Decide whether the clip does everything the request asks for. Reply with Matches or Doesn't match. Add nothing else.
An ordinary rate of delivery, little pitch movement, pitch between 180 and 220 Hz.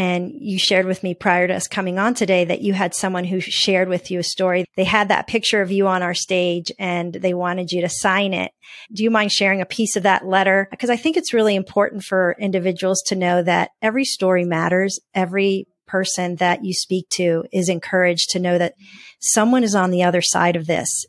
Doesn't match